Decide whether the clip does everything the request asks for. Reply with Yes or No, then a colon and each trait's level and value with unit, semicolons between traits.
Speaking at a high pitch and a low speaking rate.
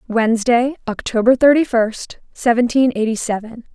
Yes: high, 235 Hz; slow, 110 wpm